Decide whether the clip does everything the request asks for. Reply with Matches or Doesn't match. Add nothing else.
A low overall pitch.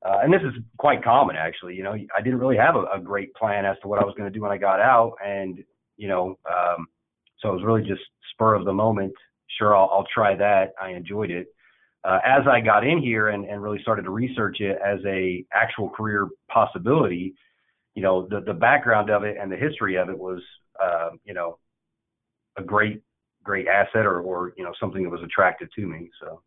Matches